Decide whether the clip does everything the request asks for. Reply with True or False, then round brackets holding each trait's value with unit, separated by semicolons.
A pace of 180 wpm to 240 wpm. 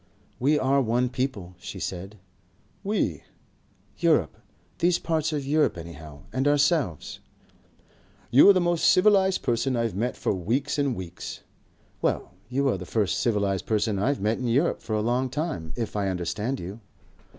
False (160 wpm)